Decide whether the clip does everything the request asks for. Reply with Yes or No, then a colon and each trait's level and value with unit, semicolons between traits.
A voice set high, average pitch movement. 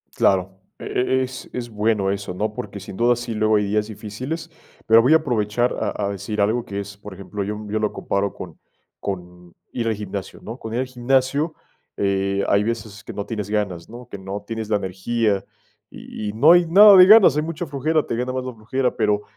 No: low, 110 Hz; average, 3.8 semitones